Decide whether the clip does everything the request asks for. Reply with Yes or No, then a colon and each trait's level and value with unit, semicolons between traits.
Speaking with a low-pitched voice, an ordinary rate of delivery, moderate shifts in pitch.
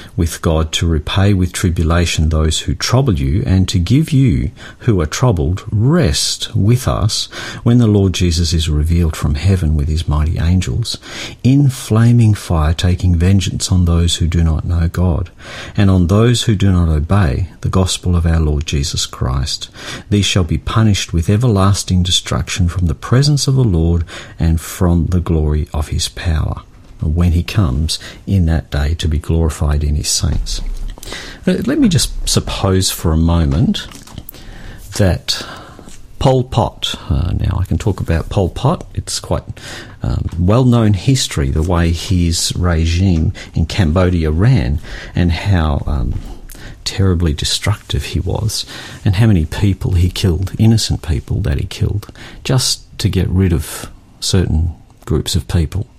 Yes: very low, 95 Hz; average, 160 wpm; average, 4.6 semitones